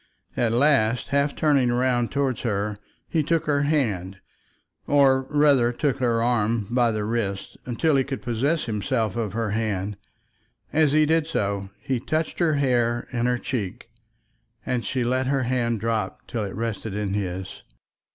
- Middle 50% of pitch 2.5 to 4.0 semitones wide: No, average, 4.4 semitones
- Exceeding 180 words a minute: No, average, 160 wpm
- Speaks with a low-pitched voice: Yes, low, 120 Hz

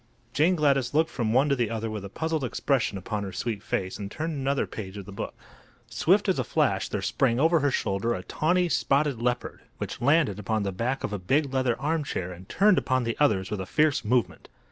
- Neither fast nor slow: No, fast, 225 wpm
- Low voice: Yes, low, 125 Hz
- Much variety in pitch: Yes, wide, 6.0 semitones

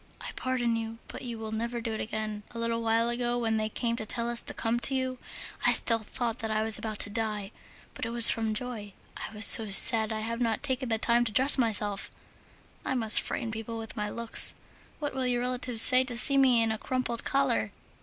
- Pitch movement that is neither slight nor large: No, narrow, 1.7 semitones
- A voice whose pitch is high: Yes, high, 230 Hz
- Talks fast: Yes, fast, 235 wpm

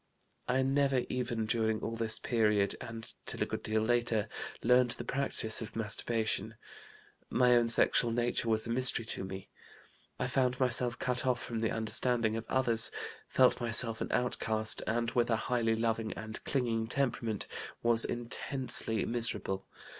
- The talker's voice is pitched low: Yes, low, 115 Hz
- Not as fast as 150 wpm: No, average, 155 wpm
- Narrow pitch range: Yes, narrow, 1.9 semitones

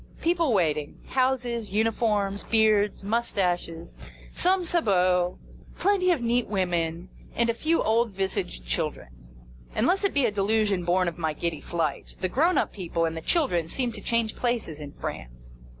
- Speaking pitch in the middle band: No, high, 205 Hz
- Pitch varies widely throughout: Yes, wide, 5.8 semitones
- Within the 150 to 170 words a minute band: Yes, average, 155 wpm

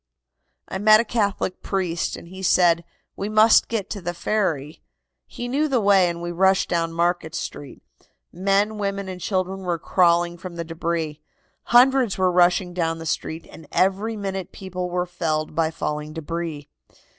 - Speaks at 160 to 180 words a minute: Yes, average, 170 wpm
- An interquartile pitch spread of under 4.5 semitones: Yes, average, 2.9 semitones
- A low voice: No, medium, 180 Hz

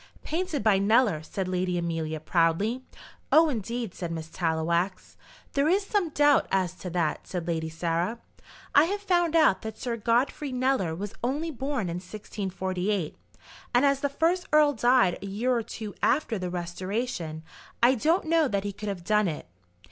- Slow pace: No, average, 170 wpm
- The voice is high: Yes, high, 210 Hz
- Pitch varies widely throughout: Yes, wide, 7.8 semitones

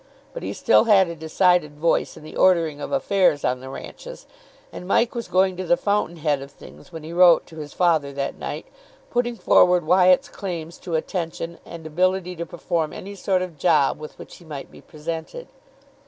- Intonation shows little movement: No, average, 3.0 semitones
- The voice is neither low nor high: Yes, medium, 170 Hz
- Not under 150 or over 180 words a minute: No, average, 200 wpm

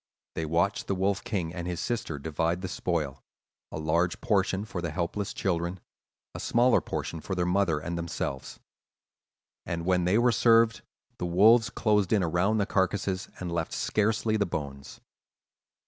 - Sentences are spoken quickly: No, average, 165 wpm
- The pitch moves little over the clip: No, average, 3.5 semitones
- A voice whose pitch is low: Yes, very low, 90 Hz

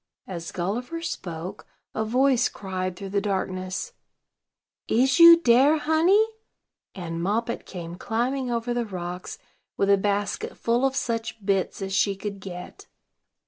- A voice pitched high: Yes, high, 205 Hz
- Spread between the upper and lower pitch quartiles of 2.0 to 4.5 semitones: No, average, 4.9 semitones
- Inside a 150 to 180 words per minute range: No, average, 140 wpm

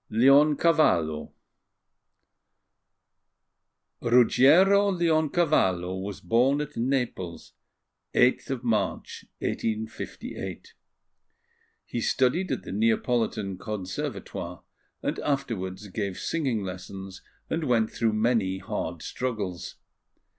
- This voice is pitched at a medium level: No, low, 115 Hz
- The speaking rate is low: Yes, slow, 80 wpm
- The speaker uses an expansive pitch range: Yes, wide, 6.4 semitones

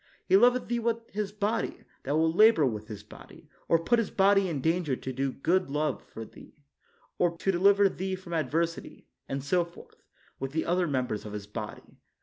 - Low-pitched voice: No, medium, 170 Hz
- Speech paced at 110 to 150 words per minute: No, average, 190 wpm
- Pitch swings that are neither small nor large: No, wide, 6.4 semitones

